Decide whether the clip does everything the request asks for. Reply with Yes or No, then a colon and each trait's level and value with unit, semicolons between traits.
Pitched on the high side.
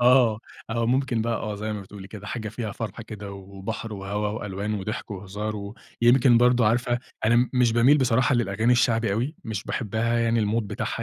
No: low, 110 Hz